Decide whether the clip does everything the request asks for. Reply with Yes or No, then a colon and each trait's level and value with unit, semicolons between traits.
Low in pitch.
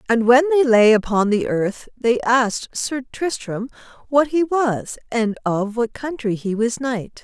No: high, 240 Hz